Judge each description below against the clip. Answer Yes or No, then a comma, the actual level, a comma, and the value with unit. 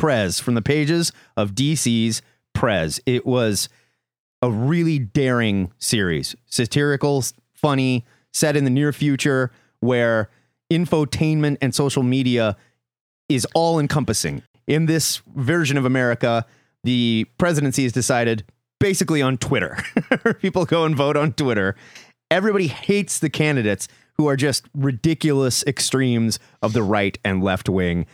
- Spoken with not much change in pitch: No, average, 4.5 semitones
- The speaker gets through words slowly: Yes, slow, 130 wpm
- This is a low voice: Yes, low, 130 Hz